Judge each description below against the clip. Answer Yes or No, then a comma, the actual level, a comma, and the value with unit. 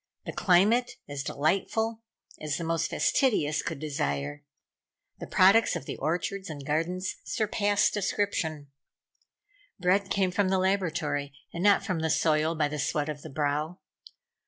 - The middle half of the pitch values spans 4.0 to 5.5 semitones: Yes, average, 4.8 semitones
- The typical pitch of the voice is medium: Yes, medium, 165 Hz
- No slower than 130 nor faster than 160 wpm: Yes, average, 145 wpm